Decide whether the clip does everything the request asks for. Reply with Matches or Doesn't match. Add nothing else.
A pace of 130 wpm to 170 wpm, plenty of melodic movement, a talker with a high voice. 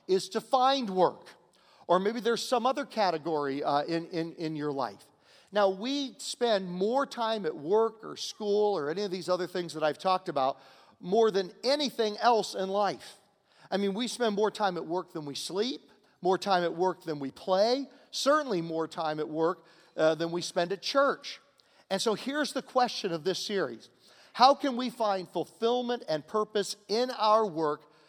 Doesn't match